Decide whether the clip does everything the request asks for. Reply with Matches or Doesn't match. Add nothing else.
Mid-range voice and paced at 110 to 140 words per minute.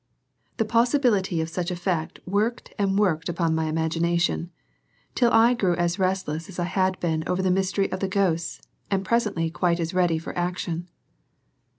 Doesn't match